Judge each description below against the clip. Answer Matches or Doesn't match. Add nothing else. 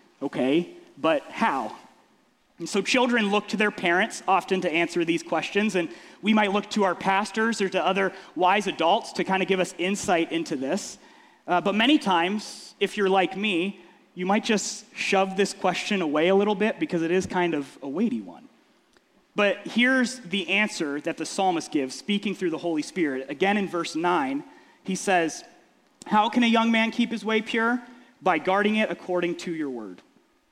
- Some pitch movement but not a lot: Matches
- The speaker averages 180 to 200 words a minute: Matches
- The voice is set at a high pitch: Matches